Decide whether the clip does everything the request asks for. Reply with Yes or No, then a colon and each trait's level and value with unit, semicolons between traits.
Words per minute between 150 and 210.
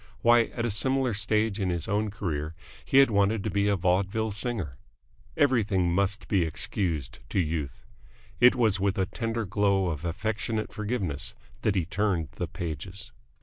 Yes: average, 165 wpm